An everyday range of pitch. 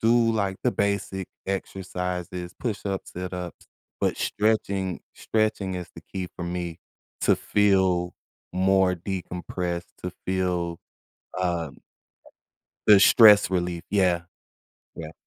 No: narrow, 2.0 semitones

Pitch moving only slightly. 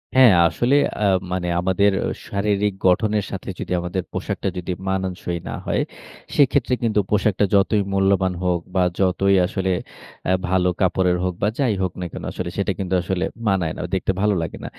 Yes: narrow, 2.1 semitones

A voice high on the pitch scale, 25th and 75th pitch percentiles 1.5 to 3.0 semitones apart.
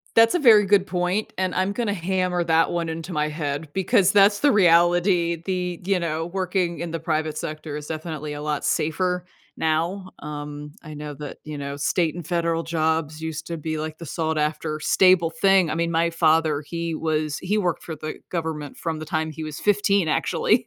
No: medium, 165 Hz; average, 2.7 semitones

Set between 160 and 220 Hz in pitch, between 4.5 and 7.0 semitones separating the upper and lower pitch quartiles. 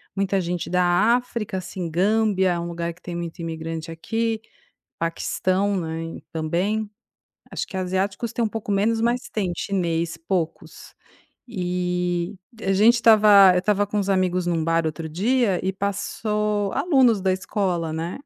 No: high, 190 Hz; average, 3.6 semitones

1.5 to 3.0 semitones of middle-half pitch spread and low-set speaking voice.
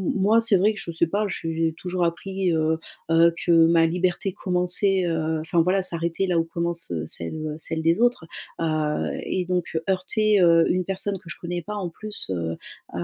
No: narrow, 2.6 semitones; medium, 170 Hz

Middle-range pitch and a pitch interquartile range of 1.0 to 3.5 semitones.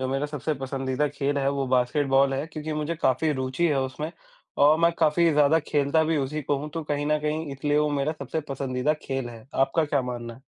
Yes: medium, 145 Hz; narrow, 2.4 semitones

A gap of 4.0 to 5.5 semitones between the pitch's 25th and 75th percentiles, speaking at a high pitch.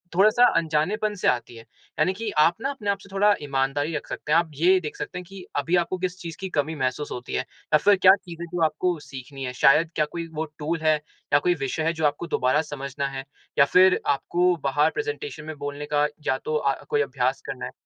No: average, 4.3 semitones; medium, 160 Hz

